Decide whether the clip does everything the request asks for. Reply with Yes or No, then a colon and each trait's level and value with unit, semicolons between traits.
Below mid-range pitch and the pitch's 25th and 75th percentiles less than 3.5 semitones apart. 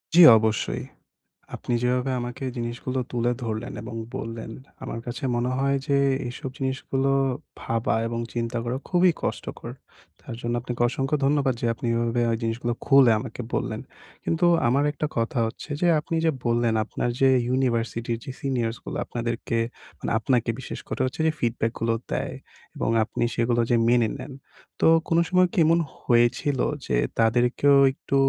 Yes: low, 120 Hz; narrow, 2.5 semitones